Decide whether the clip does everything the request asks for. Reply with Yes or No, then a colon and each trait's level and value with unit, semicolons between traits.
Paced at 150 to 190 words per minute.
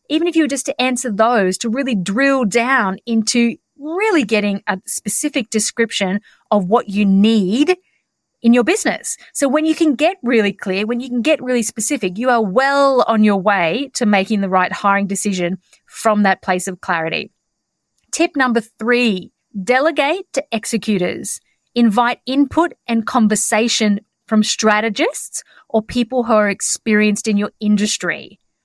Yes: average, 155 wpm